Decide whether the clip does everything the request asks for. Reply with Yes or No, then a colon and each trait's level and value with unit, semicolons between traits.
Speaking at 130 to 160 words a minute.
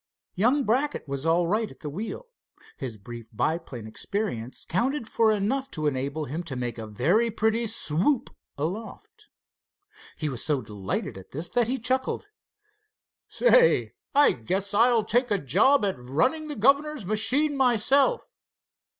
Yes: average, 150 wpm